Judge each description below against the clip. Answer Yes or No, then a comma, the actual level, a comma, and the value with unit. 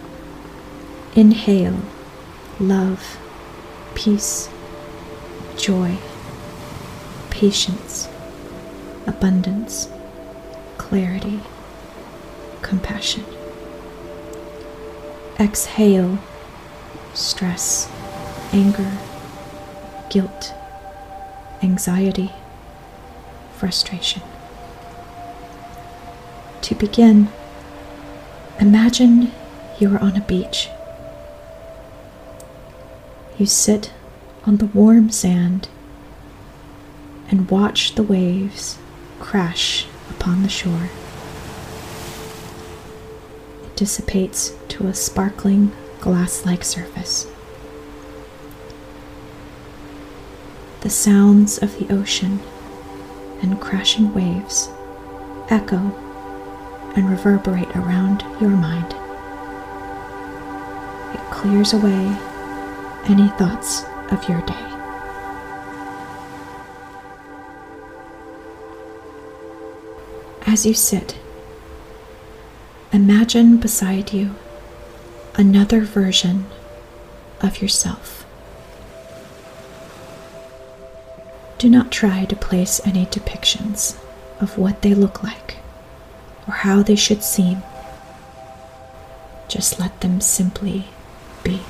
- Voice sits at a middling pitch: Yes, medium, 165 Hz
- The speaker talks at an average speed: No, slow, 65 wpm